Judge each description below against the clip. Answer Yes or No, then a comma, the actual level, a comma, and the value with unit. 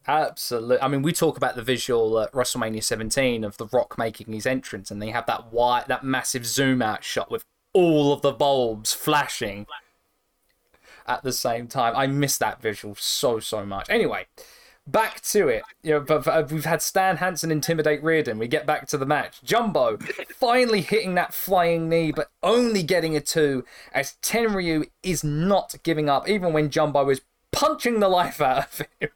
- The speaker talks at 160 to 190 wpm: Yes, average, 185 wpm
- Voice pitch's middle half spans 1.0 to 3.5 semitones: No, average, 5.2 semitones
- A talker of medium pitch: Yes, medium, 150 Hz